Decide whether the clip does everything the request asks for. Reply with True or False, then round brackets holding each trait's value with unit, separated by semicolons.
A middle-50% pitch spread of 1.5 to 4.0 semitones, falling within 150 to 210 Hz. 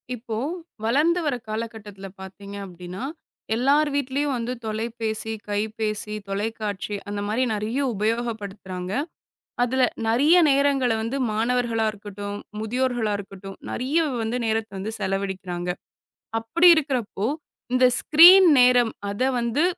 False (3.7 semitones; 225 Hz)